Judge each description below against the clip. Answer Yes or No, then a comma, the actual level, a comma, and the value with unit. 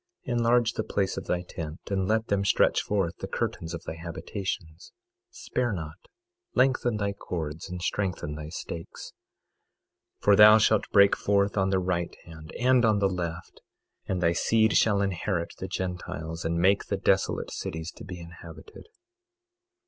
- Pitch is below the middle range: Yes, very low, 95 Hz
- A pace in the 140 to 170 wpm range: Yes, average, 165 wpm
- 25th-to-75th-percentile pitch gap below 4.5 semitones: Yes, average, 3.5 semitones